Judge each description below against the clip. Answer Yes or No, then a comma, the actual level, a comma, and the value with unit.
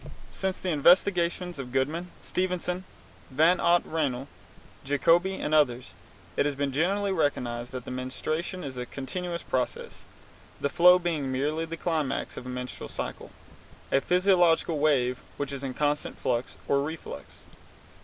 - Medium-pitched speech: Yes, medium, 150 Hz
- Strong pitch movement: No, average, 4.8 semitones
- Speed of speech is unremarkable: Yes, average, 145 wpm